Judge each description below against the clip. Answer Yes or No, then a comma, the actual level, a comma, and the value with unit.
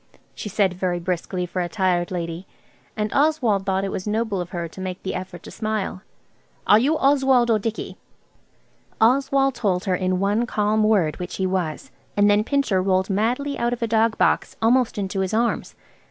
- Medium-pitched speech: No, high, 205 Hz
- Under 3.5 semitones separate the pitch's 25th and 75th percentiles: No, average, 3.9 semitones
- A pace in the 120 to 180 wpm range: No, average, 190 wpm